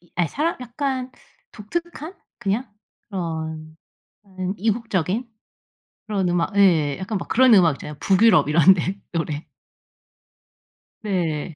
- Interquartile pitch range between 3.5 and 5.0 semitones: No, wide, 5.4 semitones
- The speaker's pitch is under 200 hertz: Yes, high, 190 Hz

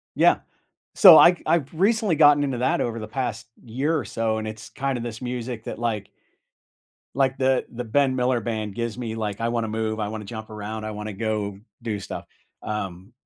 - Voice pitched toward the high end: No, low, 115 Hz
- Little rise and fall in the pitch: No, average, 3.2 semitones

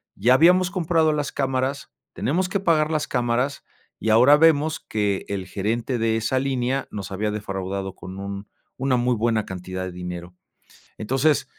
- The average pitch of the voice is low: Yes, low, 120 Hz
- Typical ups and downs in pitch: No, wide, 6.5 semitones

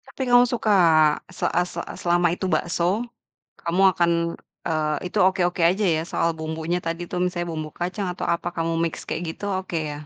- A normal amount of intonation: No, narrow, 2.0 semitones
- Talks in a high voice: No, medium, 175 Hz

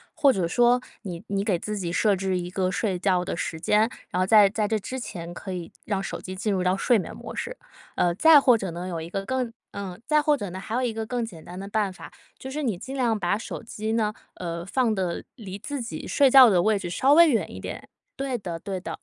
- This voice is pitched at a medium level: No, high, 205 Hz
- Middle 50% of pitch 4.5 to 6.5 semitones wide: Yes, average, 4.8 semitones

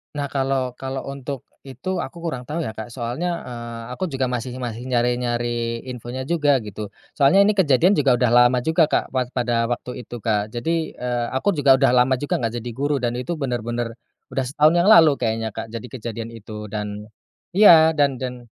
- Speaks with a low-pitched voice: Yes, low, 125 Hz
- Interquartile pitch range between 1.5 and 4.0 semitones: Yes, average, 3.3 semitones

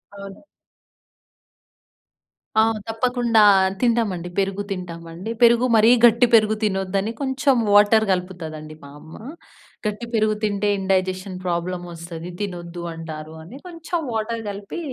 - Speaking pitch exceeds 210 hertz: No, high, 195 Hz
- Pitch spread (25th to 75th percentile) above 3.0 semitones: Yes, average, 4.2 semitones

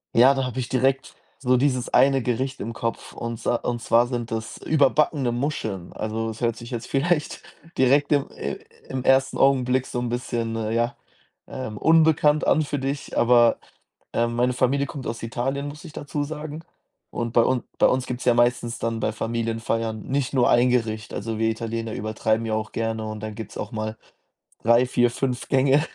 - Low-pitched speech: Yes, low, 120 Hz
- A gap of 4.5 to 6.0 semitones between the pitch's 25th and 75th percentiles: No, average, 2.9 semitones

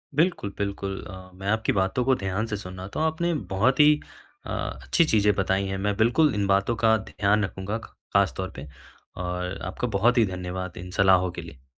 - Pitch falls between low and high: No, low, 100 Hz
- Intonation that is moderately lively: Yes, average, 3.1 semitones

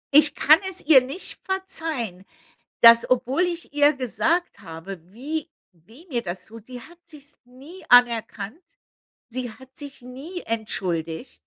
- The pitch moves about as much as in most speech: No, wide, 5.7 semitones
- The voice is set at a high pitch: Yes, very high, 255 Hz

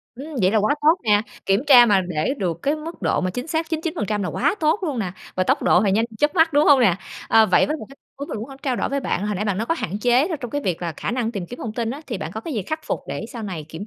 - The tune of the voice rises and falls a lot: Yes, wide, 6.6 semitones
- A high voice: Yes, high, 230 Hz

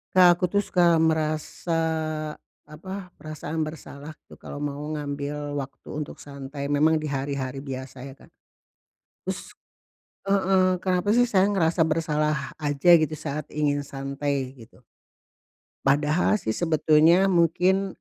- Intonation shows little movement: No, average, 3.6 semitones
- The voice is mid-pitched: Yes, medium, 155 Hz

